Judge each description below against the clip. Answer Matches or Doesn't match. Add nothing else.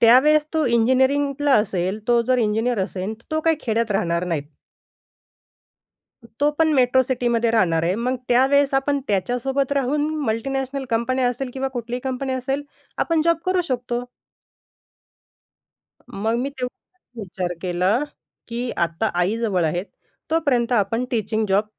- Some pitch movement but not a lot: Matches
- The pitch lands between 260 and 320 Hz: Doesn't match